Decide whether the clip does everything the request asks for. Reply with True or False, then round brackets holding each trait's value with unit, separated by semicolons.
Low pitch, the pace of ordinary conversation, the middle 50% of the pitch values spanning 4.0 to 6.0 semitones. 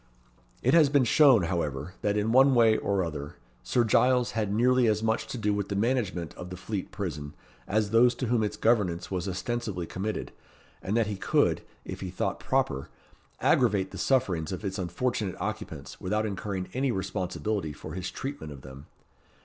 True (105 Hz; 180 wpm; 4.4 semitones)